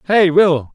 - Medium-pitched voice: Yes, medium, 170 Hz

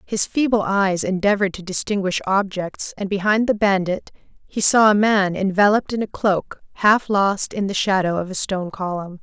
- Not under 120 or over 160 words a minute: No, average, 180 wpm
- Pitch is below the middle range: No, high, 195 Hz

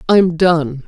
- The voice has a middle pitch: Yes, medium, 165 Hz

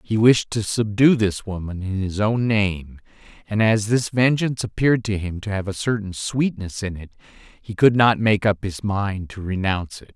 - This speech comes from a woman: No, male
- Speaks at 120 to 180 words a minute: No, average, 200 wpm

